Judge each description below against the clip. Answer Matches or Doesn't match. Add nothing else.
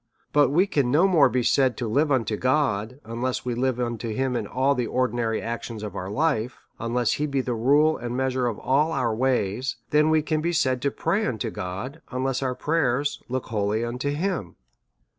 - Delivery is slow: Doesn't match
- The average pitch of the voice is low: Matches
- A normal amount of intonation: Matches